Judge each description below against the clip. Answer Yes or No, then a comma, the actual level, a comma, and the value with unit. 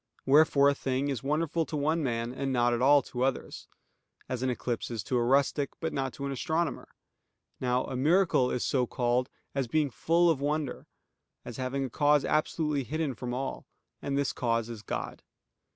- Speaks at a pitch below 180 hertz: Yes, low, 135 Hz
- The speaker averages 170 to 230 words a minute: Yes, average, 190 wpm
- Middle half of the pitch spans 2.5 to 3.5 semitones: Yes, average, 3.0 semitones